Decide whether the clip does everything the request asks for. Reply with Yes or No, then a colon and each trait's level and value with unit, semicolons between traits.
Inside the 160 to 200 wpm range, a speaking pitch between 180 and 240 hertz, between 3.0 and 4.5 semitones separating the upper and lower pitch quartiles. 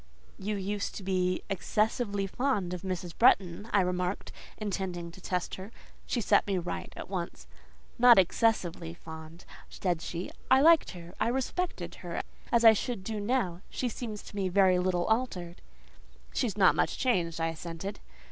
Yes: average, 165 wpm; high, 190 Hz; average, 3.9 semitones